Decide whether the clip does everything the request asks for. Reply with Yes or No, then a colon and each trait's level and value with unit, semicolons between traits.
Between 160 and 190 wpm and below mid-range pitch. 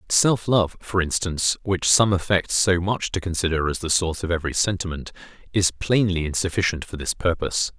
Yes: average, 175 wpm; very low, 90 Hz